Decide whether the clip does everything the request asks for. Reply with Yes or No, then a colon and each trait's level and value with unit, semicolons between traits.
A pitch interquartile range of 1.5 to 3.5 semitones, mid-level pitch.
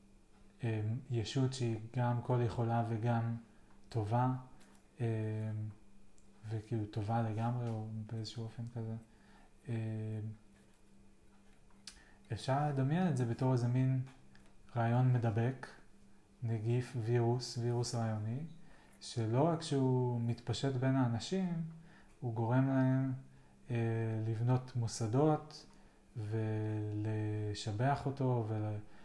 No: average, 2.8 semitones; low, 115 Hz